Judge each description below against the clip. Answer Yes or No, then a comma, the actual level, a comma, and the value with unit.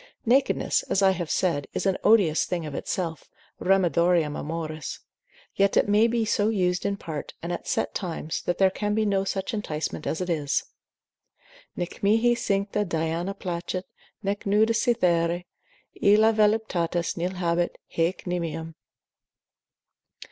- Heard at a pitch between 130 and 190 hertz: Yes, medium, 185 Hz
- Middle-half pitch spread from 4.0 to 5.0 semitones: No, average, 3.5 semitones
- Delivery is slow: No, average, 145 wpm